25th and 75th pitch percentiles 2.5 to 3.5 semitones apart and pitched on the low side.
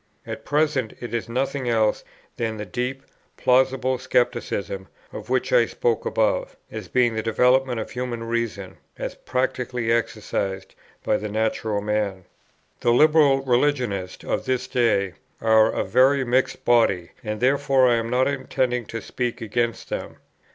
Yes: average, 2.9 semitones; low, 120 Hz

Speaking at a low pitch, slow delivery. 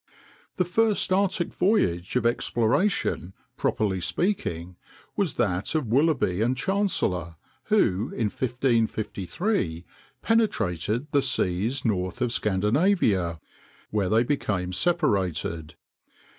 Yes: low, 115 Hz; slow, 100 wpm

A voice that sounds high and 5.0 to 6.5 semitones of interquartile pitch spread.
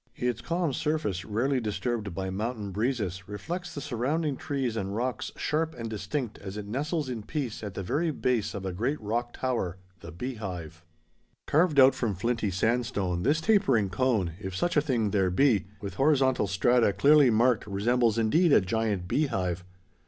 No: low, 115 Hz; wide, 5.5 semitones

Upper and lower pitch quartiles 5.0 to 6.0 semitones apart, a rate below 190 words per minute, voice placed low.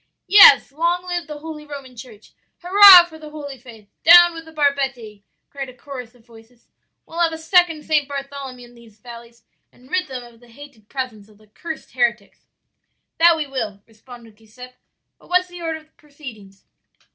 No: wide, 5.4 semitones; average, 180 wpm; very high, 275 Hz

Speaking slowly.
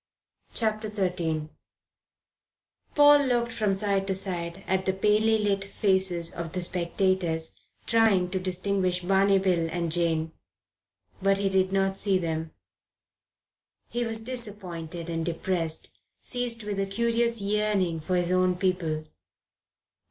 Yes: slow, 130 wpm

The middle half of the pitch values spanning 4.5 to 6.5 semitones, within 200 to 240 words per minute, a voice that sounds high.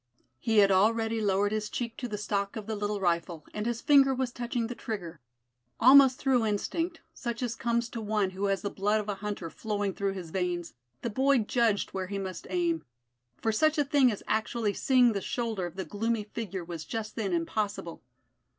No: average, 3.4 semitones; fast, 205 wpm; high, 210 Hz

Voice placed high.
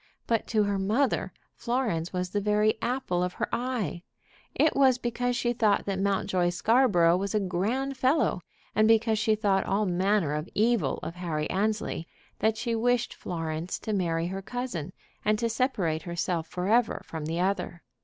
Yes: high, 205 Hz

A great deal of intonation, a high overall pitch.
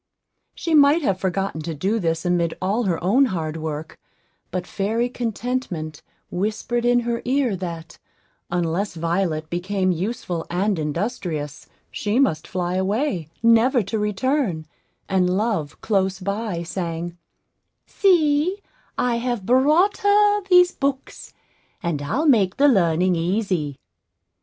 Yes: wide, 6.2 semitones; high, 195 Hz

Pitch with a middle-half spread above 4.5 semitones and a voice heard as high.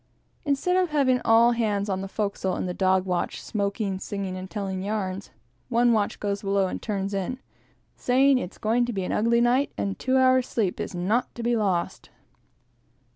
No: average, 3.9 semitones; high, 210 Hz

